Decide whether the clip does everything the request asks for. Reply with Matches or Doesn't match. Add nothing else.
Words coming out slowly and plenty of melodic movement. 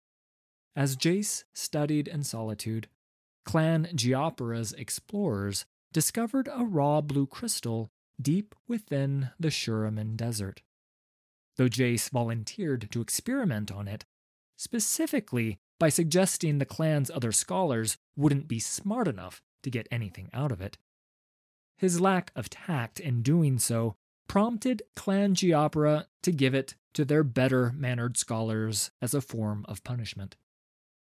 Matches